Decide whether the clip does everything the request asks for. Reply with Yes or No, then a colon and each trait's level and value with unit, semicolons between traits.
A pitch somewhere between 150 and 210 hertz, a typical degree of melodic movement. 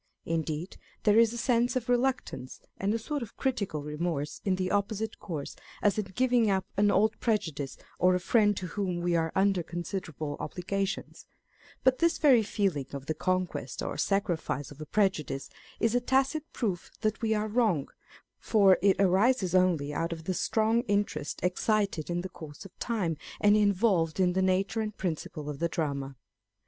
Yes: high, 190 Hz; average, 4.7 semitones